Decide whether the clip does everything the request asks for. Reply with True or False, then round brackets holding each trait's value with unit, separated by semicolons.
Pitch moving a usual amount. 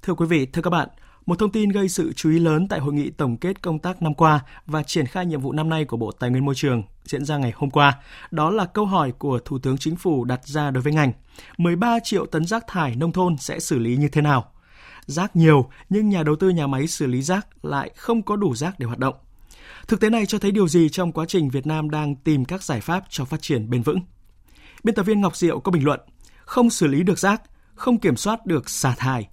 True (4.8 semitones)